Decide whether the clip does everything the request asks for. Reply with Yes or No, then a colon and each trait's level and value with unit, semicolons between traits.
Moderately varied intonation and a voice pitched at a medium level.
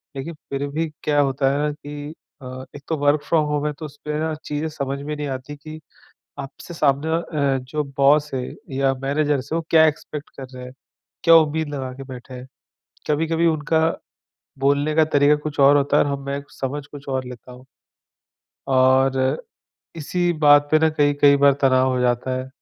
No: narrow, 2.1 semitones; medium, 145 Hz